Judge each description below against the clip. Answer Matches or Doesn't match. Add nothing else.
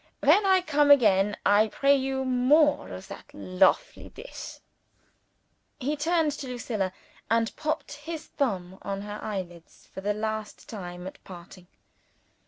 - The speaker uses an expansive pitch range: Matches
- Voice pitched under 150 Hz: Doesn't match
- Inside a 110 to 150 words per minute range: Matches